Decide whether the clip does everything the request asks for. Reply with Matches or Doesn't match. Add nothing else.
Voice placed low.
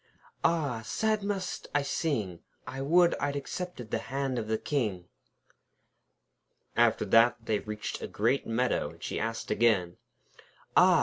Matches